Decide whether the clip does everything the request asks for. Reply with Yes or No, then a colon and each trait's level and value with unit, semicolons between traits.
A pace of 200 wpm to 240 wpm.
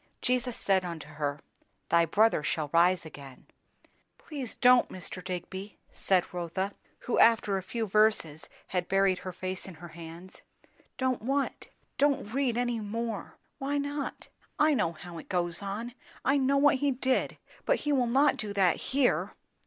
No: average, 165 wpm